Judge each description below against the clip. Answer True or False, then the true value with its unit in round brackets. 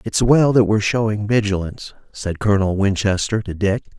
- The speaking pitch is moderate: False (105 Hz)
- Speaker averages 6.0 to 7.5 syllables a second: False (5.5 syllables/s)